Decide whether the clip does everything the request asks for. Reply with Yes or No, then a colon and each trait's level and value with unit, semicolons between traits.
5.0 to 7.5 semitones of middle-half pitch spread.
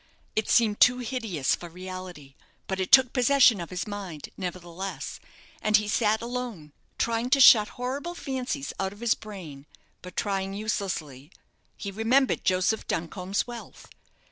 No: average, 4.6 semitones